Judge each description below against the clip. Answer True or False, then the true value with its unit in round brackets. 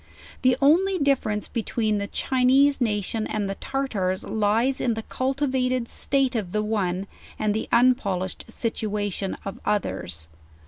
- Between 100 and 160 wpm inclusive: True (140 wpm)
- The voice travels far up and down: False (4.1 semitones)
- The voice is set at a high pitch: True (220 Hz)